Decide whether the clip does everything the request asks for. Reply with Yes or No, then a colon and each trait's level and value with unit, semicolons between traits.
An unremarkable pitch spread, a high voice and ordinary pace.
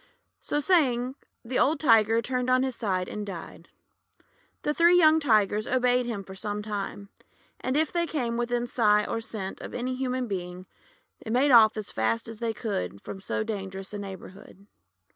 Yes: average, 4.1 semitones; high, 225 Hz; average, 175 wpm